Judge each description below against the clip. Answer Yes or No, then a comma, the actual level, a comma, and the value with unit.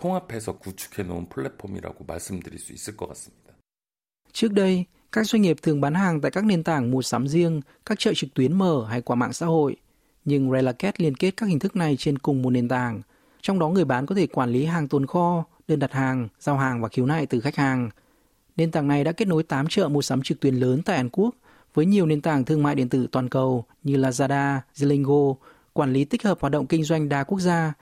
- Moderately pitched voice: Yes, medium, 145 Hz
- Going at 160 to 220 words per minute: Yes, average, 215 wpm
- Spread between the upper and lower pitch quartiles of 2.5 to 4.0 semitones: No, average, 4.5 semitones